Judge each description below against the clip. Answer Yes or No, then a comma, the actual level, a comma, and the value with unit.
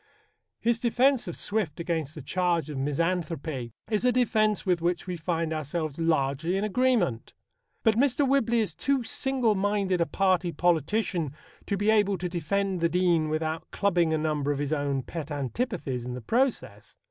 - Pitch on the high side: No, medium, 175 Hz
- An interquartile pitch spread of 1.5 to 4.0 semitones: No, wide, 5.4 semitones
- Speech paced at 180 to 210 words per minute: No, average, 170 wpm